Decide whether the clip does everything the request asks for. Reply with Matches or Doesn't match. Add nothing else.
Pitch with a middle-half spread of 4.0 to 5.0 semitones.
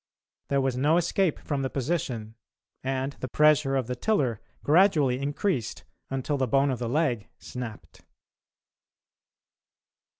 Doesn't match